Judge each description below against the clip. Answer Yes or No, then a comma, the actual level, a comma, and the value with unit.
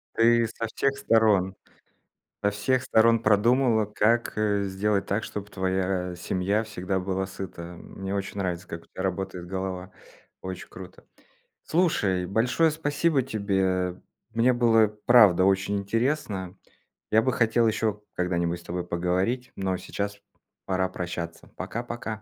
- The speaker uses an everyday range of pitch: Yes, average, 3.5 semitones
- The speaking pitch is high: No, low, 100 Hz